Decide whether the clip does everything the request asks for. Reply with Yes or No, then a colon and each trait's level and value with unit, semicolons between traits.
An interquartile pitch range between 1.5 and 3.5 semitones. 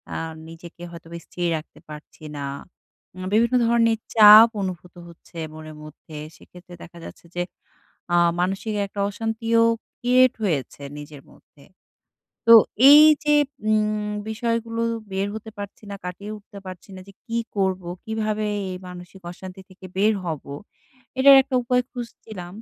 No: average, 4.2 semitones